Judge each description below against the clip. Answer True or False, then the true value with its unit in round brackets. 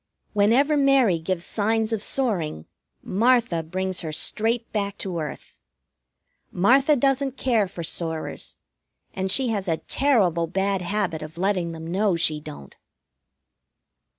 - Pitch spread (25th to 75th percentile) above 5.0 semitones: True (5.5 semitones)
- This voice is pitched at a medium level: False (195 Hz)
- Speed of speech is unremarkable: False (130 wpm)